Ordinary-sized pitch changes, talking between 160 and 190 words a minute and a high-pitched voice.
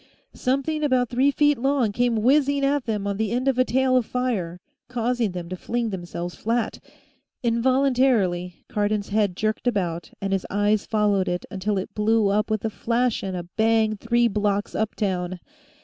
Yes: average, 4.1 semitones; average, 175 wpm; high, 220 Hz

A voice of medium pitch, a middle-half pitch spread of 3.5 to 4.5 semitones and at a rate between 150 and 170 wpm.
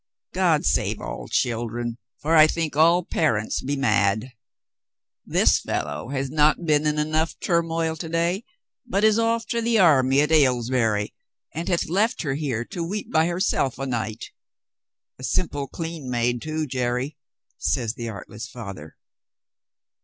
No: medium, 145 Hz; wide, 5.4 semitones; average, 155 wpm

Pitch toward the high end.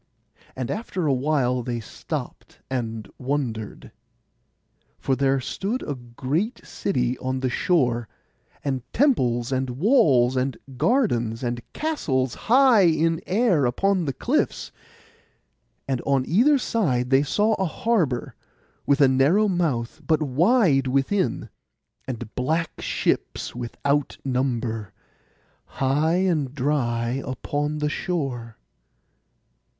No: low, 135 Hz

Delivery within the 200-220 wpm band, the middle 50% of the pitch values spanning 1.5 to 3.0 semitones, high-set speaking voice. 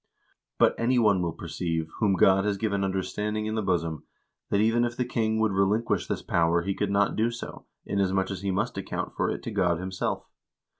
No: fast, 205 wpm; average, 2.7 semitones; low, 100 Hz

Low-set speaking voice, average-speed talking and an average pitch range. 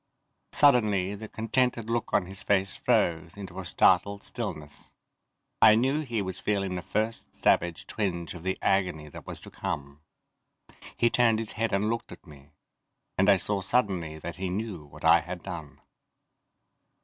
Yes: very low, 95 Hz; average, 165 wpm; average, 4.0 semitones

